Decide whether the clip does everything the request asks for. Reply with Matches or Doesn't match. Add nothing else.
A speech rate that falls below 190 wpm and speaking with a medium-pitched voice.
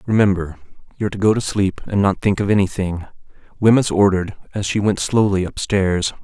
Doesn't match